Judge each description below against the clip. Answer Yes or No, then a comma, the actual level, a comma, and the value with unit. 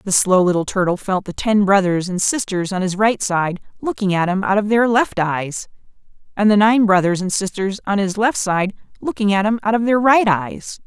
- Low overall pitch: No, high, 200 Hz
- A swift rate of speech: Yes, fast, 220 wpm